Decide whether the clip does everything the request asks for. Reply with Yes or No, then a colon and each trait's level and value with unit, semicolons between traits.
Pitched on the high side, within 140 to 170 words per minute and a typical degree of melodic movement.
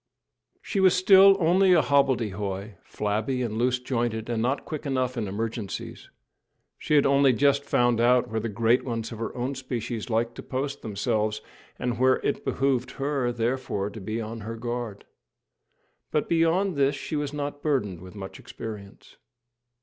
No: low, 120 Hz; average, 165 wpm; average, 3.9 semitones